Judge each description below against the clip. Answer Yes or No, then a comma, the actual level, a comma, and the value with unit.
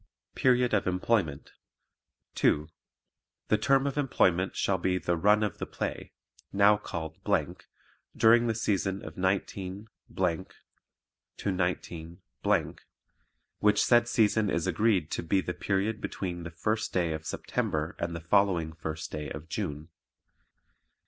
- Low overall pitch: Yes, very low, 95 Hz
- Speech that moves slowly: Yes, slow, 130 wpm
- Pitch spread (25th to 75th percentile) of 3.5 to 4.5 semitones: Yes, average, 4.1 semitones